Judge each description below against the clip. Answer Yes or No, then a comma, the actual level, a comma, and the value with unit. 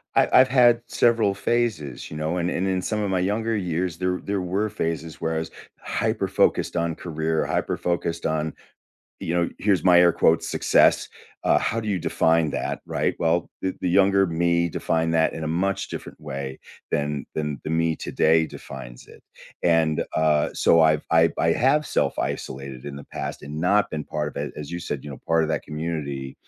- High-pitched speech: No, very low, 85 Hz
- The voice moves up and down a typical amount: Yes, average, 3.2 semitones